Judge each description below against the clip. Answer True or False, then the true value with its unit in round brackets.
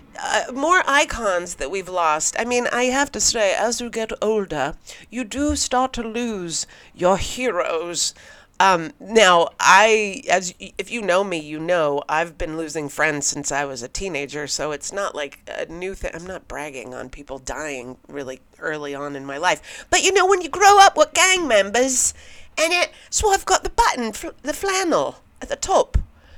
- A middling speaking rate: True (195 wpm)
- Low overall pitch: False (195 Hz)